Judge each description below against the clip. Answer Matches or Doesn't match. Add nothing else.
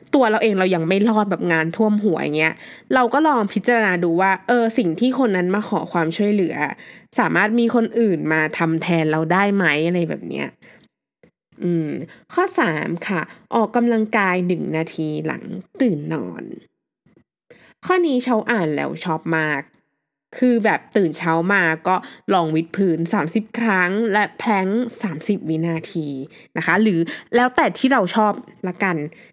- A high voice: Matches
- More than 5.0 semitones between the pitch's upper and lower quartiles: Matches